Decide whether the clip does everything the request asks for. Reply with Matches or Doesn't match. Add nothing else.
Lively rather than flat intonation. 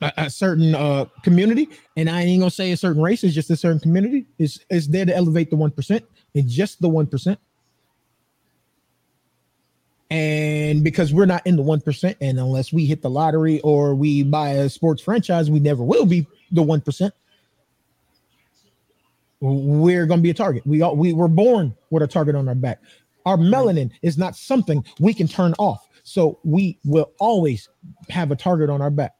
Doesn't match